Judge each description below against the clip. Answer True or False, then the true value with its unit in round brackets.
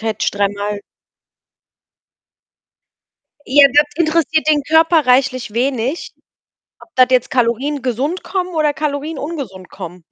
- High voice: True (275 Hz)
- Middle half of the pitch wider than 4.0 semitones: True (4.9 semitones)